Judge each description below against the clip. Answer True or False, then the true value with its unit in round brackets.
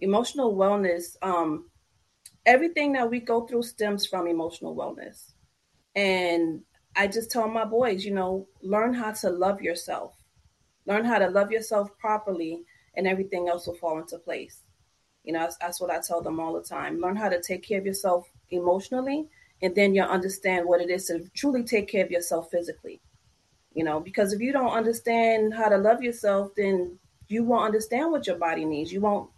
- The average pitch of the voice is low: False (195 Hz)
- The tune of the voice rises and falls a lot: False (4.2 semitones)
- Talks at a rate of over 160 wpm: True (190 wpm)